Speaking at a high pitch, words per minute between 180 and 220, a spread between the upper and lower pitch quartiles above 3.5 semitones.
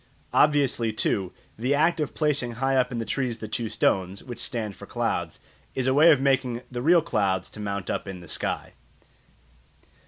No: low, 120 Hz; average, 185 wpm; average, 4.6 semitones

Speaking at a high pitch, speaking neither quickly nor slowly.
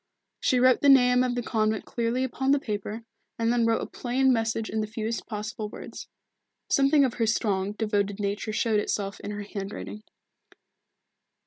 Yes: high, 225 Hz; average, 175 wpm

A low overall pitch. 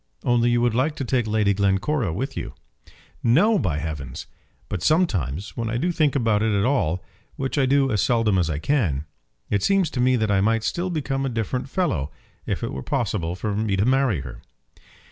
Yes: low, 115 Hz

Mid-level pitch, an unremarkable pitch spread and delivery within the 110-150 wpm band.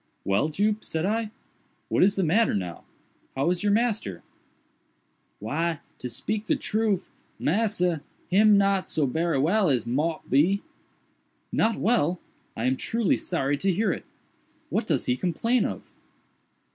No: medium, 180 Hz; wide, 6.4 semitones; average, 145 wpm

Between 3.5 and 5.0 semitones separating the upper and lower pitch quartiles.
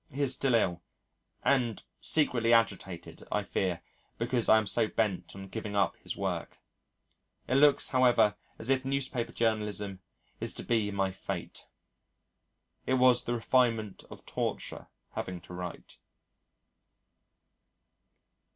Yes: average, 4.1 semitones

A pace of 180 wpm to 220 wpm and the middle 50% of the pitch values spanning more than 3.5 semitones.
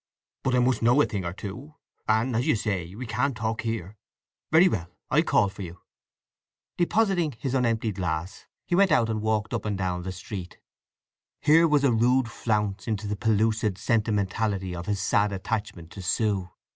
Yes: average, 185 wpm; average, 4.1 semitones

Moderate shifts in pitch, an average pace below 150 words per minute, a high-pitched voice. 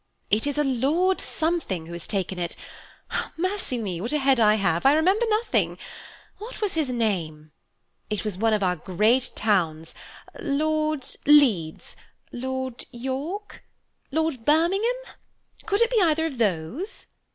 No: wide, 8.1 semitones; average, 140 wpm; very high, 260 Hz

